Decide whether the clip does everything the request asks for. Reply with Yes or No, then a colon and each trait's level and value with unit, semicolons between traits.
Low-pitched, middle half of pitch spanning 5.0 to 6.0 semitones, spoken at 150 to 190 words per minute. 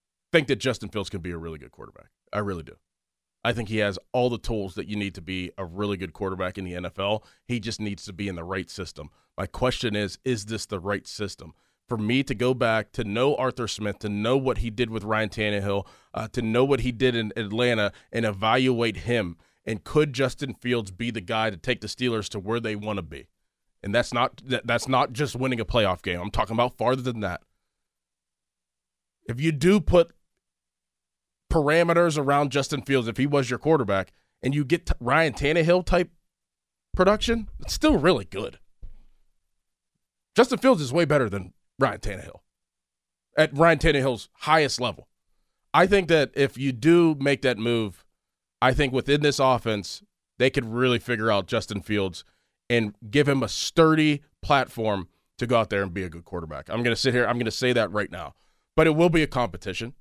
No: low, 115 Hz; average, 5.3 semitones; average, 200 wpm